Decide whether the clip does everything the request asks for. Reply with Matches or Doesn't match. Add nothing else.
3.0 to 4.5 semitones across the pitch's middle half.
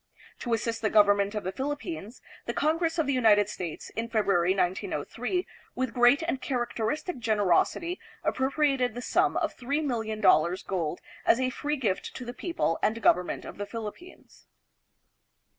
Doesn't match